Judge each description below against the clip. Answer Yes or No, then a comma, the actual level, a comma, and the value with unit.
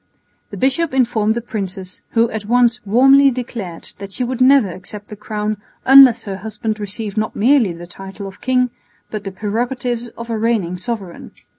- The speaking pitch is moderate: No, high, 220 Hz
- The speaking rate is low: No, average, 175 wpm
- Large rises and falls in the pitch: No, average, 3.7 semitones